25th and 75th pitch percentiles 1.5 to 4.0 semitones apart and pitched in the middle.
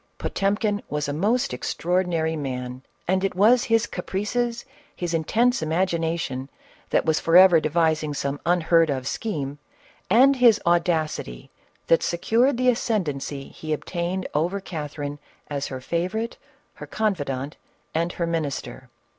No: average, 5.3 semitones; medium, 170 Hz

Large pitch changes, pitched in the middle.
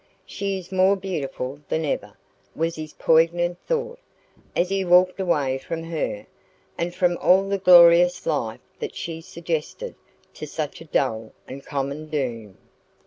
No: average, 4.0 semitones; medium, 165 Hz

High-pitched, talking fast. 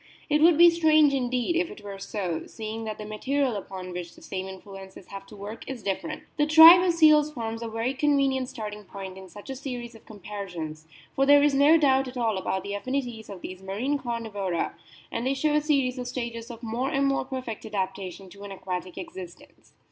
Yes: high, 230 Hz; fast, 210 wpm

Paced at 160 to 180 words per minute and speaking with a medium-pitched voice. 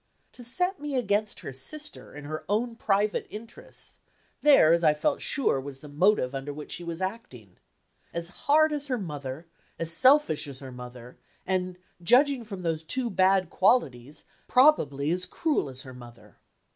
Yes: average, 170 wpm; medium, 180 Hz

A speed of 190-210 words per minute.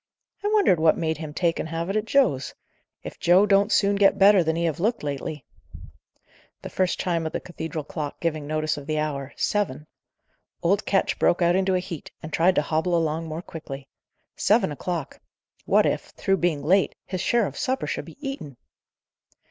Yes: average, 195 wpm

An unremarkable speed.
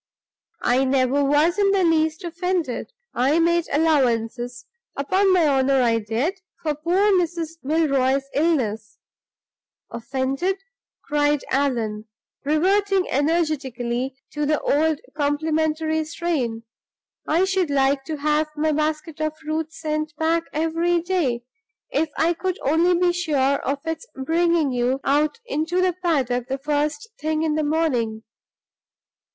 No: slow, 130 wpm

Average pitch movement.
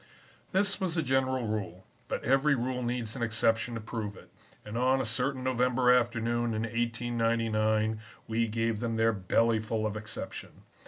No: narrow, 2.3 semitones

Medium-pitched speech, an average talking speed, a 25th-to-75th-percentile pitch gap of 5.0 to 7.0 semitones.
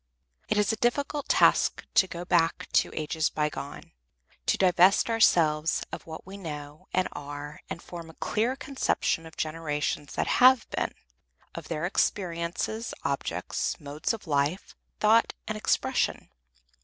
Yes: medium, 170 Hz; average, 145 wpm; wide, 5.6 semitones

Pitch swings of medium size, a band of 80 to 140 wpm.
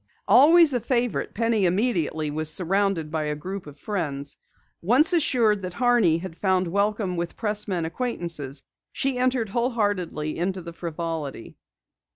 No: wide, 6.0 semitones; slow, 135 wpm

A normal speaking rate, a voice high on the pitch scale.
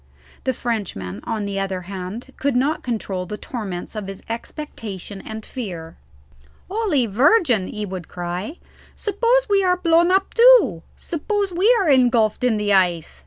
Yes: average, 155 wpm; high, 225 Hz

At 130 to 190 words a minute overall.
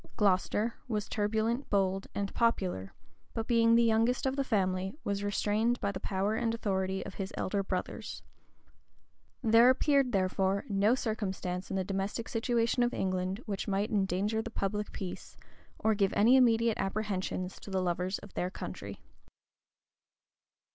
Yes: average, 150 wpm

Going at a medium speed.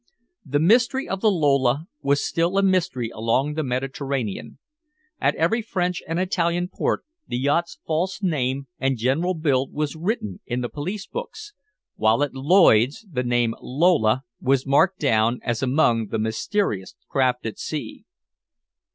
Yes: average, 150 wpm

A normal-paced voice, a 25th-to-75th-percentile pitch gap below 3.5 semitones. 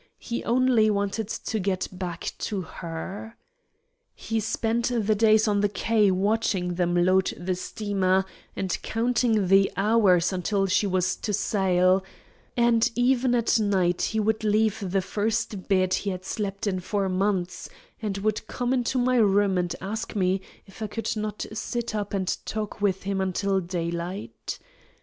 Yes: average, 160 wpm; average, 2.9 semitones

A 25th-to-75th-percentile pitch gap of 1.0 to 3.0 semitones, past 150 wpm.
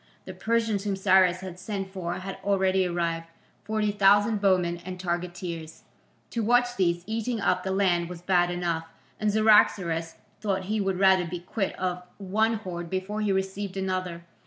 Yes: average, 2.7 semitones; average, 165 wpm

